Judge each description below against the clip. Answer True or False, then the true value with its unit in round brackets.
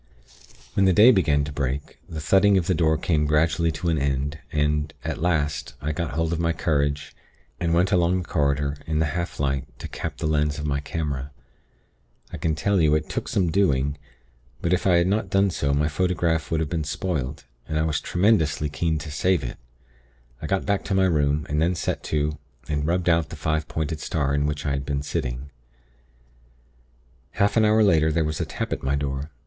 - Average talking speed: False (210 wpm)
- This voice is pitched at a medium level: False (80 Hz)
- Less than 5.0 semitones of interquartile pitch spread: True (3.0 semitones)